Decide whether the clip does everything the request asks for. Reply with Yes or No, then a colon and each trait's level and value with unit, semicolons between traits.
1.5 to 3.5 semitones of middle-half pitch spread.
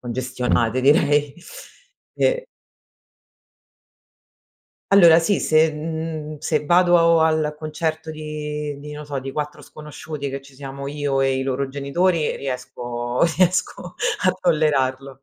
Yes: average, 2.8 semitones